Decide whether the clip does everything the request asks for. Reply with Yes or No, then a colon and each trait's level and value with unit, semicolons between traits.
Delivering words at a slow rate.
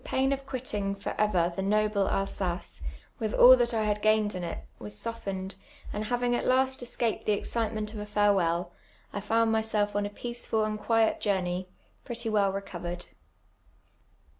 No: average, 170 wpm